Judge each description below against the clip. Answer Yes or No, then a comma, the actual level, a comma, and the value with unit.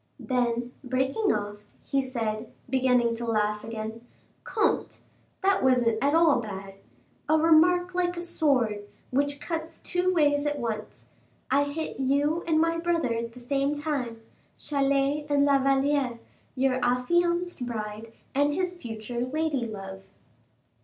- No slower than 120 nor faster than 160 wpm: Yes, average, 140 wpm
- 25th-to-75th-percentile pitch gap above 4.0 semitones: Yes, average, 5.1 semitones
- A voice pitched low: No, very high, 270 Hz